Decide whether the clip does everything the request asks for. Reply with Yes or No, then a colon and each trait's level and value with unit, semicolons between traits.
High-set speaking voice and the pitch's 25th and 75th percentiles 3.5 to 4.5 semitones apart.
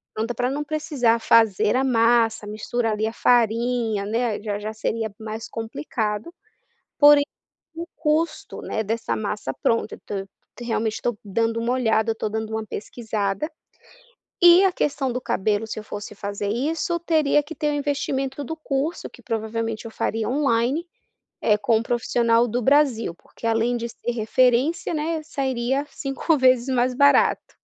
Yes: high, 235 Hz; average, 4.0 semitones